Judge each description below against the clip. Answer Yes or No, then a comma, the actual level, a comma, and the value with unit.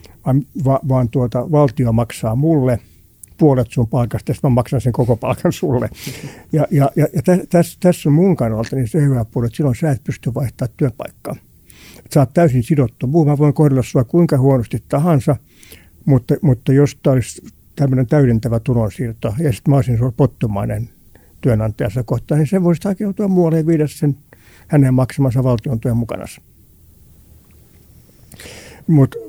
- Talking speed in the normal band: No, fast, 160 wpm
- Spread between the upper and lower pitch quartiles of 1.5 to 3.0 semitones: No, average, 4.2 semitones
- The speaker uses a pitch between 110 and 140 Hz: Yes, low, 130 Hz